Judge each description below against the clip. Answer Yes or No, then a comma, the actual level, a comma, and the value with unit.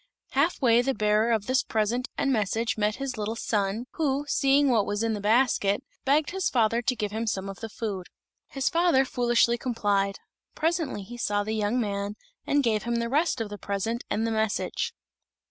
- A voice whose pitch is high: Yes, high, 230 Hz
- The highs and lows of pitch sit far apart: No, average, 3.9 semitones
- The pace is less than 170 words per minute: No, average, 195 wpm